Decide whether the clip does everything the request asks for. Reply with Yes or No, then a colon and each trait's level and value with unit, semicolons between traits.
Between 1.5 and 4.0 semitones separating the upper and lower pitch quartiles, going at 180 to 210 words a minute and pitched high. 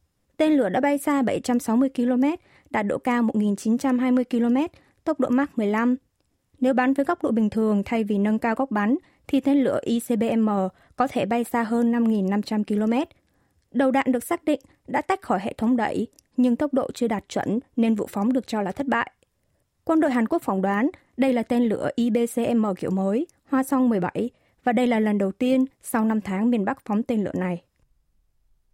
Yes: average, 3.5 semitones; average, 200 wpm; high, 240 Hz